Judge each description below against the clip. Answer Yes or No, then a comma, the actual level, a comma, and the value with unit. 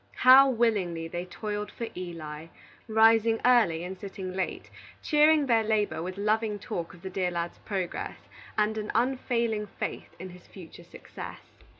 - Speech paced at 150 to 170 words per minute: Yes, average, 155 wpm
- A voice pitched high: Yes, high, 205 Hz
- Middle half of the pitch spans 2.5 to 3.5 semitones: No, average, 4.0 semitones